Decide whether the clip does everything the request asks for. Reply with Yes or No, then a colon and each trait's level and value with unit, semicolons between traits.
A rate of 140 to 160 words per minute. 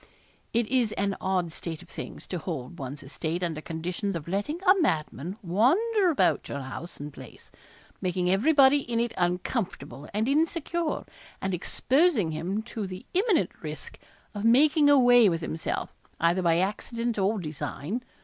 Yes: average, 155 wpm